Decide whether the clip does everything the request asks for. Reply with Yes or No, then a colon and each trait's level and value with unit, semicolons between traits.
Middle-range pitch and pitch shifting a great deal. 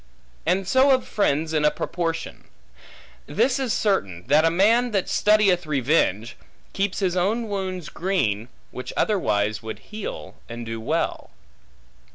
Yes: medium, 180 Hz; wide, 8.2 semitones